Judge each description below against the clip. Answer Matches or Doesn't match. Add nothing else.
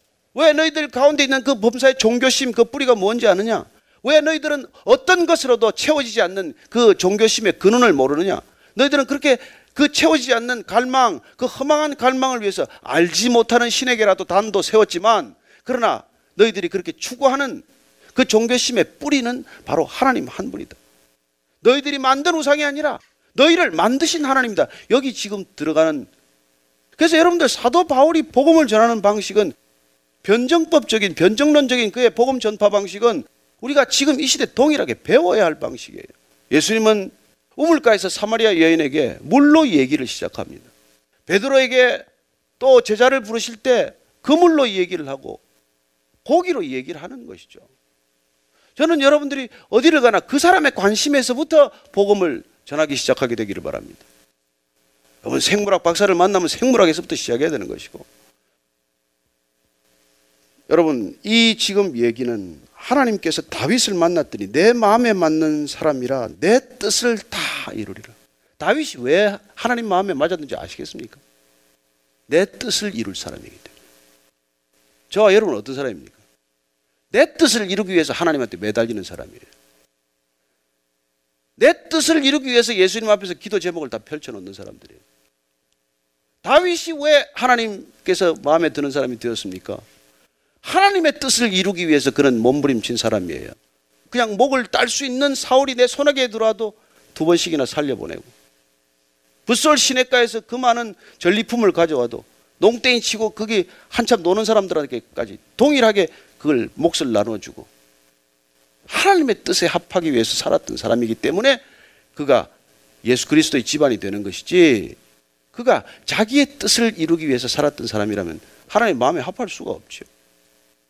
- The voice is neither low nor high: Doesn't match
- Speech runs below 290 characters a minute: Doesn't match